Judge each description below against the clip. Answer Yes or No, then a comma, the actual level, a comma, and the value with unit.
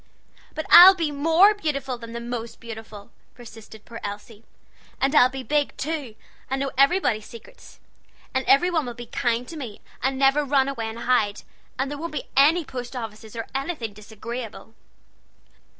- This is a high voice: Yes, very high, 255 Hz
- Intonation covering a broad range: No, average, 4.2 semitones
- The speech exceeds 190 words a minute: No, average, 165 wpm